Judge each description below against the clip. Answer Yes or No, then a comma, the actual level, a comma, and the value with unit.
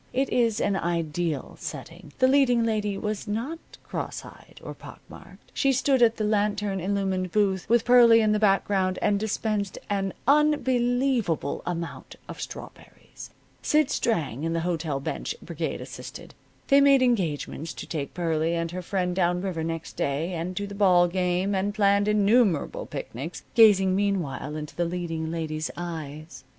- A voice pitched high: Yes, high, 195 Hz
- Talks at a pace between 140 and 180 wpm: Yes, average, 160 wpm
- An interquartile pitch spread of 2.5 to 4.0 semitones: No, average, 4.6 semitones